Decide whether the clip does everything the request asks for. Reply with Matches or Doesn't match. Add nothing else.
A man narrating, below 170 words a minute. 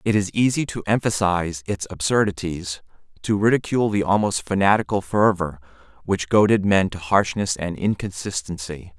Matches